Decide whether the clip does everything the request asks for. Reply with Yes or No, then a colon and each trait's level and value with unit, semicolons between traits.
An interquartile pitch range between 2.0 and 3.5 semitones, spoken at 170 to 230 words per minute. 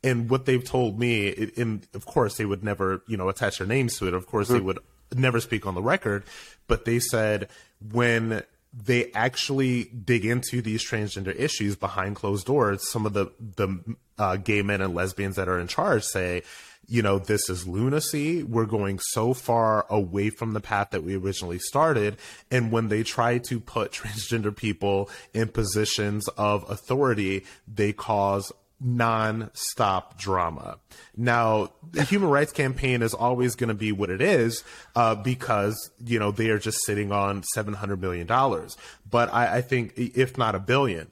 Yes: average, 3.1 semitones; average, 175 wpm